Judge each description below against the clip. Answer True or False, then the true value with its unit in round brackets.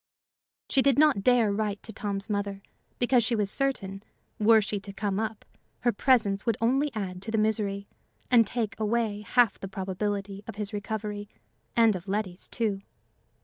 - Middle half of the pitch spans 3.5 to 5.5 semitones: False (2.5 semitones)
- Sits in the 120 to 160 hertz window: False (210 Hz)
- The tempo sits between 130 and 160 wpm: False (170 wpm)